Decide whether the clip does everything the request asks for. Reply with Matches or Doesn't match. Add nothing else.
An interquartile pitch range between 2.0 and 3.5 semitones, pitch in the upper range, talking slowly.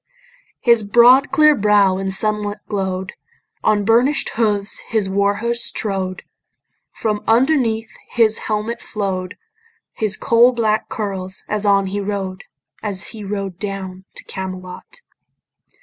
Matches